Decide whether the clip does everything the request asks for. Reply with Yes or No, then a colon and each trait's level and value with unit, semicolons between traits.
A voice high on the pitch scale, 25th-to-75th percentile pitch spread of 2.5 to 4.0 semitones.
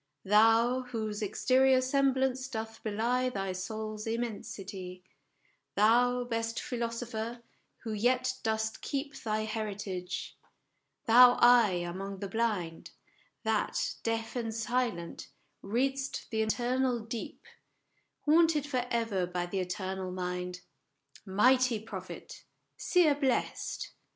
Yes: high, 225 Hz; average, 3.6 semitones